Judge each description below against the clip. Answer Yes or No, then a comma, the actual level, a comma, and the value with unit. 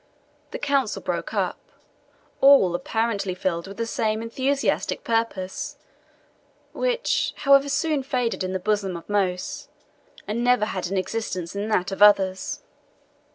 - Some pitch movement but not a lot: No, wide, 6.1 semitones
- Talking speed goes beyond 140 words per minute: No, slow, 135 wpm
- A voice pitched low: No, high, 215 Hz